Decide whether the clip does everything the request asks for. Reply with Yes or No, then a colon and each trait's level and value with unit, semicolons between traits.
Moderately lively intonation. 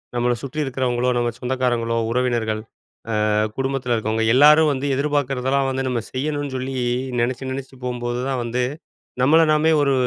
No: narrow, 2.1 semitones